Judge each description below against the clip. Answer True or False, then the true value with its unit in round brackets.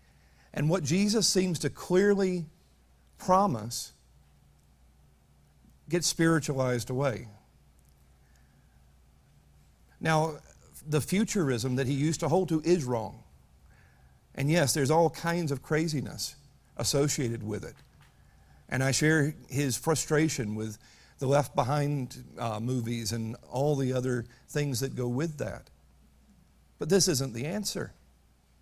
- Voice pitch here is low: True (125 Hz)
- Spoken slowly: True (115 wpm)